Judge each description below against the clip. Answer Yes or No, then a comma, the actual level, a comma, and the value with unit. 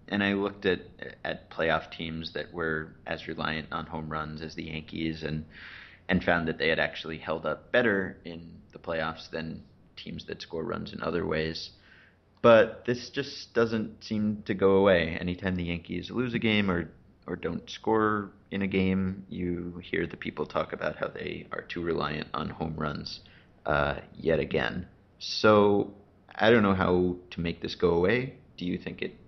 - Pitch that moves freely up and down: No, average, 3.9 semitones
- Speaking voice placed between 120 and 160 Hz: No, very low, 90 Hz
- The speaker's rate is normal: Yes, average, 185 wpm